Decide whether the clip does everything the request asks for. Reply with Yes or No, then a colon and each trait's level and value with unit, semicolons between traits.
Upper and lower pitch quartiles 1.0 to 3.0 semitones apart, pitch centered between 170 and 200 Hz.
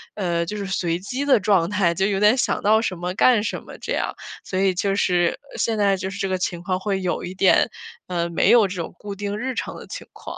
Yes: narrow, 2.5 semitones; high, 195 Hz